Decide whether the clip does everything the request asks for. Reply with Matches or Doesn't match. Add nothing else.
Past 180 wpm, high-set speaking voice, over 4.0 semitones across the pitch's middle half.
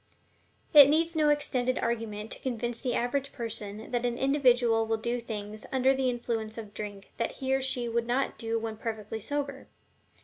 Doesn't match